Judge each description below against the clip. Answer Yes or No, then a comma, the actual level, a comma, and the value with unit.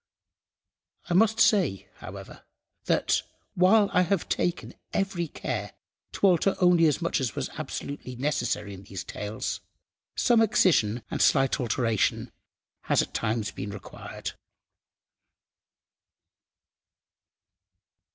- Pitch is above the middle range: No, medium, 150 Hz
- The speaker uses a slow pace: Yes, slow, 110 wpm